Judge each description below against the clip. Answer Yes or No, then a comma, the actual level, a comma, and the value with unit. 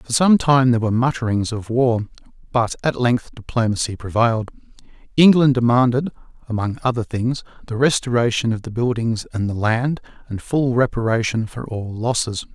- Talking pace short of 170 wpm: Yes, average, 155 wpm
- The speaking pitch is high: No, low, 120 Hz